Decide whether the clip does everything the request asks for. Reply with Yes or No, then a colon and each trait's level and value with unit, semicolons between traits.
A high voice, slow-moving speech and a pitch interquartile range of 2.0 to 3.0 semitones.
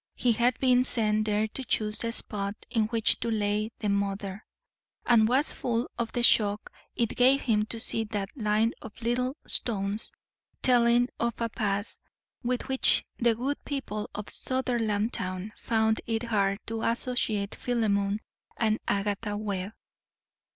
No: high, 220 Hz; average, 150 wpm; narrow, 2.4 semitones